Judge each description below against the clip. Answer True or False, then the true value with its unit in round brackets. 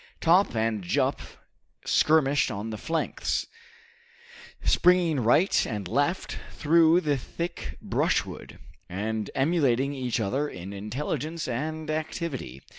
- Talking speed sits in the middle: False (110 wpm)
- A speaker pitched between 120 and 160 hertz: True (140 Hz)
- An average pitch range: False (6.3 semitones)